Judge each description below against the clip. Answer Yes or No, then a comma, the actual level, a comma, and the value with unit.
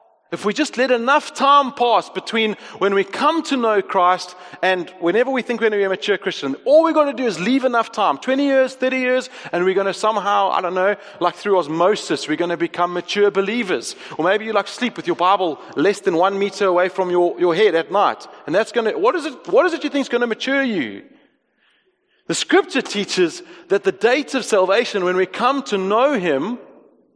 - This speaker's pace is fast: Yes, fast, 230 wpm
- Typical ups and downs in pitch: No, wide, 5.9 semitones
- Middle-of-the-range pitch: No, high, 210 Hz